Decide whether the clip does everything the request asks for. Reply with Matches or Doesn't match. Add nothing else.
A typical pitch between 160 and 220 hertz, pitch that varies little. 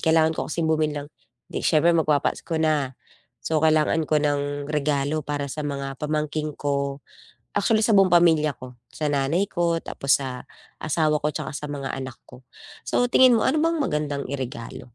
Doesn't match